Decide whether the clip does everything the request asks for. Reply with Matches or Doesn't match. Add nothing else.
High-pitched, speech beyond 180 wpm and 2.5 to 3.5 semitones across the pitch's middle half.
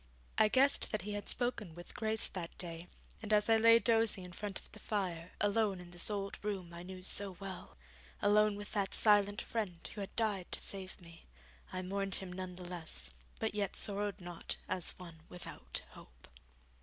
Matches